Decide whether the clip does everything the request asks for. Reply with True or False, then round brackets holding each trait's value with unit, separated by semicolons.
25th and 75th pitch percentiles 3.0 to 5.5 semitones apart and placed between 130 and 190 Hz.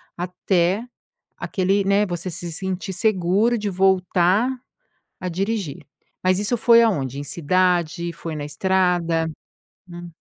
False (2.5 semitones; 185 Hz)